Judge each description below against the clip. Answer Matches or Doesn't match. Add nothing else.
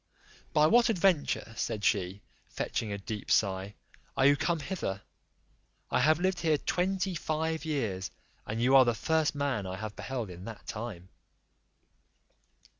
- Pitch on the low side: Matches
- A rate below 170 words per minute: Matches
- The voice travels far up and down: Matches